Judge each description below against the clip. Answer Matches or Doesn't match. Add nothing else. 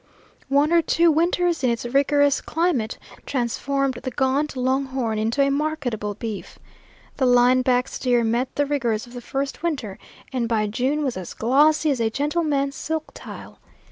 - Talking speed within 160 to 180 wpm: Matches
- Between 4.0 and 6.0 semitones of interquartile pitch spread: Doesn't match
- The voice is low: Doesn't match